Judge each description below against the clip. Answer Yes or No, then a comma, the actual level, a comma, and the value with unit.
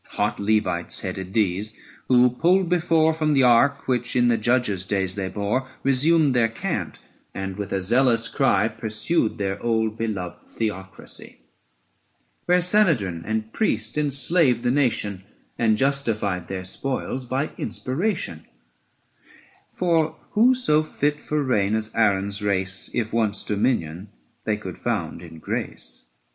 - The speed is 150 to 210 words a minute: No, average, 140 wpm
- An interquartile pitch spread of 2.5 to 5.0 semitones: No, wide, 5.6 semitones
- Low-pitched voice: Yes, low, 115 Hz